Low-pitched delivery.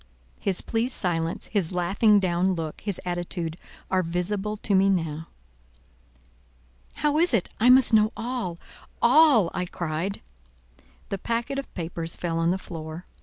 No: medium, 185 Hz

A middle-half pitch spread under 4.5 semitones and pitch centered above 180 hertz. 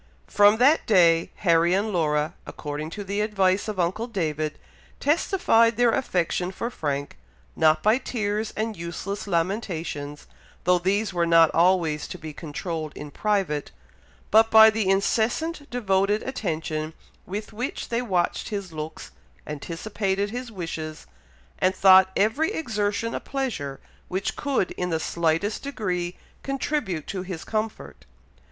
No: average, 4.8 semitones; high, 190 Hz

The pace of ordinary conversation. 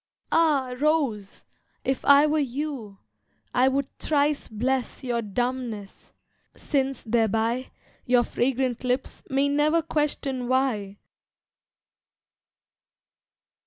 No: slow, 90 wpm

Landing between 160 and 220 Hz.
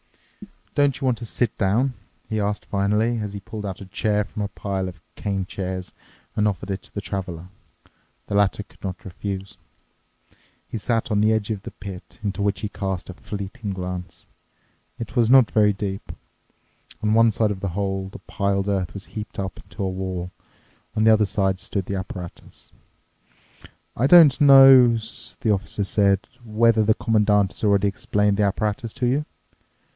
No: low, 100 Hz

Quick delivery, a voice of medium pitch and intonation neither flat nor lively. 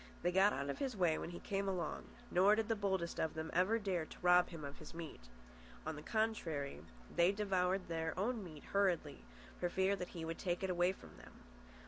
Yes: fast, 215 wpm; medium, 180 Hz; average, 3.3 semitones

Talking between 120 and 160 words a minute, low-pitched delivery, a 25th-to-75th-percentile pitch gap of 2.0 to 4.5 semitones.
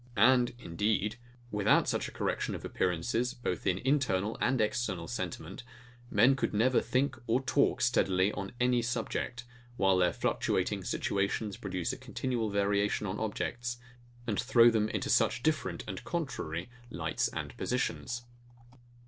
Yes: average, 140 wpm; low, 110 Hz; average, 3.9 semitones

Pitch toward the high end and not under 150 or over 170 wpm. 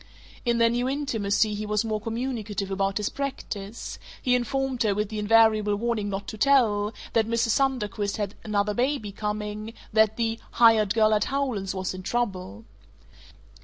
Yes: high, 215 Hz; average, 165 wpm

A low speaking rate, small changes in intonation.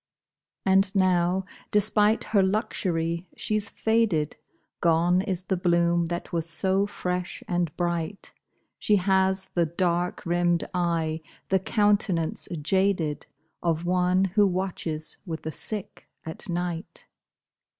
Yes: slow, 120 wpm; narrow, 2.2 semitones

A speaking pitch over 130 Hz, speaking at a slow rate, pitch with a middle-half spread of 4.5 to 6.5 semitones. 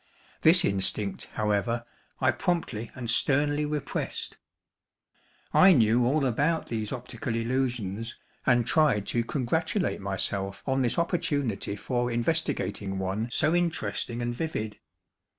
No: low, 120 Hz; slow, 115 wpm; average, 5.2 semitones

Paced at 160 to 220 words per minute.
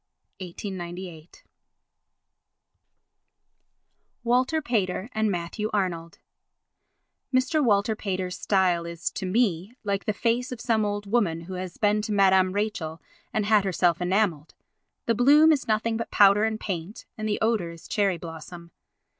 No: average, 140 wpm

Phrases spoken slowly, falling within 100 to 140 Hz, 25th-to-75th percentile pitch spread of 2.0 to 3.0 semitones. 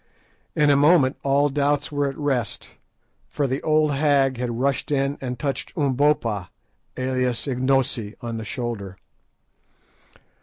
Yes: slow, 130 wpm; low, 135 Hz; narrow, 2.6 semitones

